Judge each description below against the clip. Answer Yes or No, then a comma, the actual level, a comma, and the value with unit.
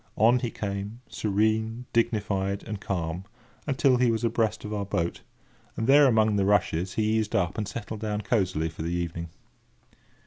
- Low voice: Yes, low, 105 Hz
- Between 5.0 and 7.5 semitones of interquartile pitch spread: No, average, 2.7 semitones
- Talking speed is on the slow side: No, average, 170 wpm